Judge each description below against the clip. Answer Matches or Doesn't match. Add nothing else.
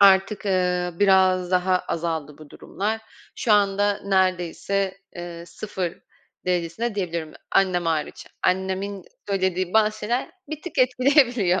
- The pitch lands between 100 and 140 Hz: Doesn't match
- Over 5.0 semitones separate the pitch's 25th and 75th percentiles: Doesn't match